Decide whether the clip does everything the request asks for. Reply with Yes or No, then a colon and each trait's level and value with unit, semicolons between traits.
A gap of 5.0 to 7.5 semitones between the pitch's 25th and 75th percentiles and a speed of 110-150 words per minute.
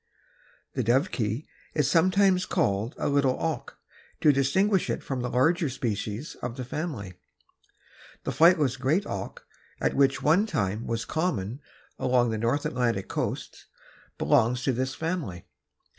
Yes: wide, 5.5 semitones; average, 140 wpm